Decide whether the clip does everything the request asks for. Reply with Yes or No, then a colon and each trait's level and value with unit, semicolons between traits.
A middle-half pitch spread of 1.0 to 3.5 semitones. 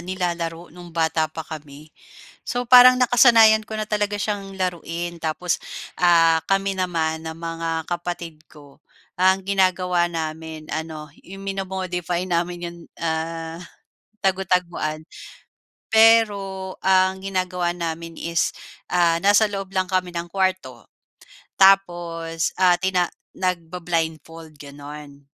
Yes: average, 2.7 semitones